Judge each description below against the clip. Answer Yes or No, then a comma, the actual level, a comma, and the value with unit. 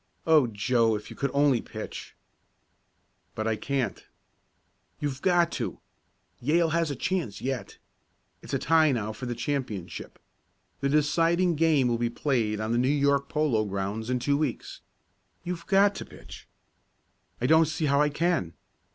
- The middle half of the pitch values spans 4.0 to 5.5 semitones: Yes, average, 5.2 semitones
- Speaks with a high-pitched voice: No, medium, 140 Hz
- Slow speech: No, average, 160 wpm